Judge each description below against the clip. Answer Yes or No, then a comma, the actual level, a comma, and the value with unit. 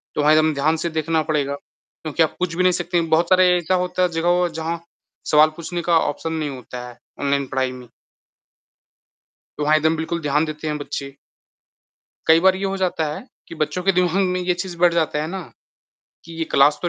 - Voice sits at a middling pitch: Yes, medium, 160 Hz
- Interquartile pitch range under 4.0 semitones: Yes, average, 2.9 semitones